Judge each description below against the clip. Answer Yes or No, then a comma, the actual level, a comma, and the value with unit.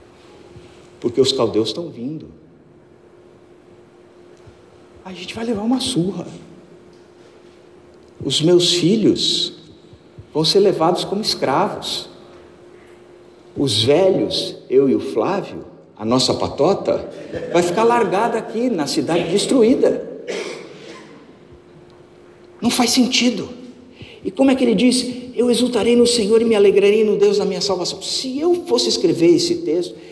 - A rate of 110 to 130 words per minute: Yes, average, 125 wpm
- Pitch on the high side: Yes, high, 225 Hz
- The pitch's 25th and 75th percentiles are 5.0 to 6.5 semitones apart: Yes, wide, 5.5 semitones